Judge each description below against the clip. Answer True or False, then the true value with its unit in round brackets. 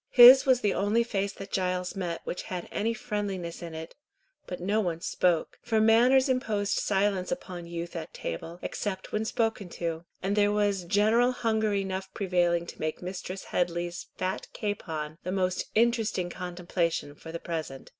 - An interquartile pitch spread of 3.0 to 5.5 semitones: True (3.6 semitones)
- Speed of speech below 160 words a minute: False (165 wpm)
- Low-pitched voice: False (190 Hz)